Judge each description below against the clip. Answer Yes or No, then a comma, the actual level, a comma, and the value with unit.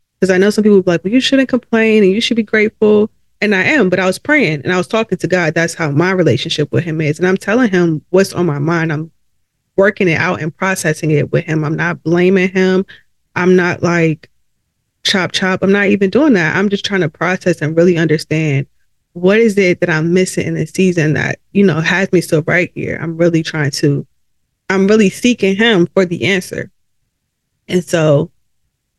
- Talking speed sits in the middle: No, fast, 220 wpm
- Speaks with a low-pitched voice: No, medium, 180 Hz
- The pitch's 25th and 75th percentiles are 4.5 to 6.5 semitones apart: No, average, 3.2 semitones